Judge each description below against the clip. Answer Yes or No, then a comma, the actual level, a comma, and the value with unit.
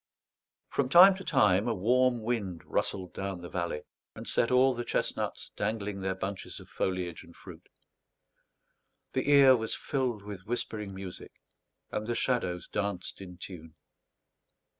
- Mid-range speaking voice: No, low, 105 Hz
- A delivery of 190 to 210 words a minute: No, average, 145 wpm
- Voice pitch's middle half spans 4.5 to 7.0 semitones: Yes, average, 4.8 semitones